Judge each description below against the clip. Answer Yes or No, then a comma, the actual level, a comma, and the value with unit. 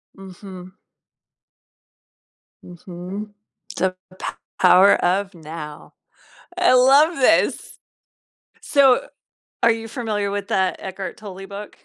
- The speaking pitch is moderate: No, high, 200 Hz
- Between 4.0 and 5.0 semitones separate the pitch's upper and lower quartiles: No, average, 3.5 semitones